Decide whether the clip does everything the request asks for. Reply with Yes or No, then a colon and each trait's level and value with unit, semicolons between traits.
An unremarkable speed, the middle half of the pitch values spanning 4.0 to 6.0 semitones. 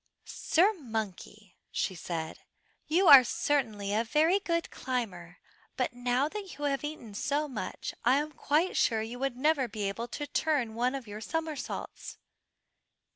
Yes: average, 155 wpm; wide, 5.5 semitones